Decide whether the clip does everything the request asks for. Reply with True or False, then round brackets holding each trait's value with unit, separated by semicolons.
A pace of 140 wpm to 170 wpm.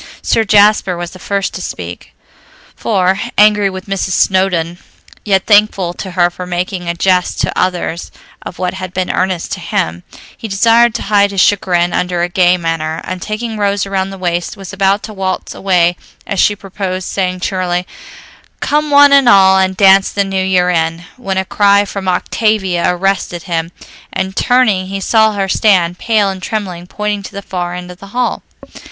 False (185 wpm)